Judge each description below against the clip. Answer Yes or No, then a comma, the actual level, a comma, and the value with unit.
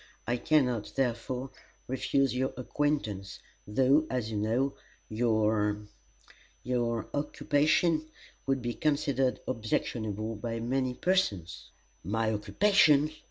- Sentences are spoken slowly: Yes, slow, 105 wpm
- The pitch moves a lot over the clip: No, average, 4.2 semitones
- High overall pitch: No, low, 125 Hz